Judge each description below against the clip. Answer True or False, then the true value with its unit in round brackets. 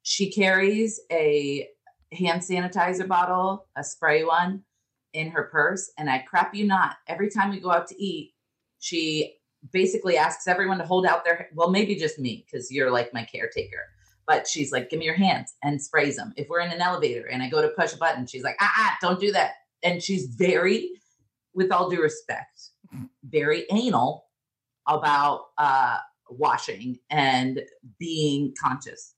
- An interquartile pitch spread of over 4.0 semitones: True (4.5 semitones)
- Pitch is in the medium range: True (170 Hz)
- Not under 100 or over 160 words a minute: False (175 wpm)